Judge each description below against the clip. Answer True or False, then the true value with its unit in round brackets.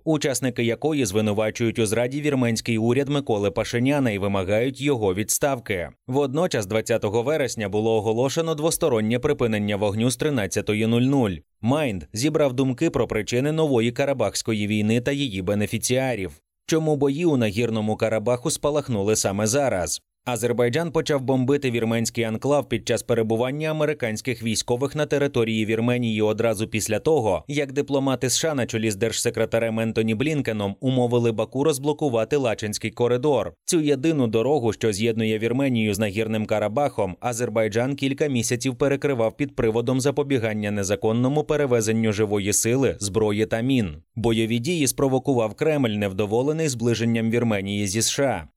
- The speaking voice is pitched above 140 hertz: False (120 Hz)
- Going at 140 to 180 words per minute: False (130 wpm)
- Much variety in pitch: False (4.1 semitones)